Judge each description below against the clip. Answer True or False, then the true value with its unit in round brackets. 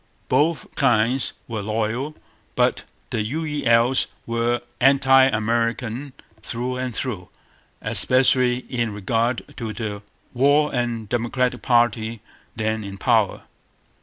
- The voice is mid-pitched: False (120 Hz)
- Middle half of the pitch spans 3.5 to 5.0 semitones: False (2.7 semitones)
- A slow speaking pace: True (105 wpm)